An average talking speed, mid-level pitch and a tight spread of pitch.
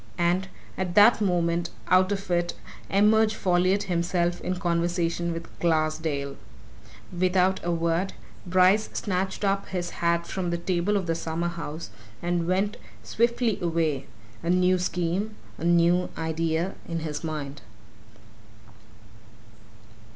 No: slow, 125 wpm; medium, 175 Hz; narrow, 2.0 semitones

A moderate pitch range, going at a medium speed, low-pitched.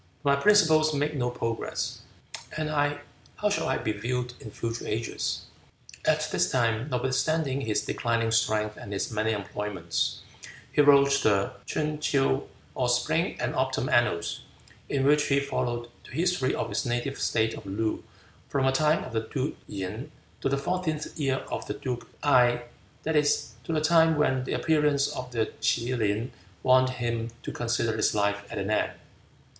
Yes: average, 4.3 semitones; average, 170 wpm; low, 130 Hz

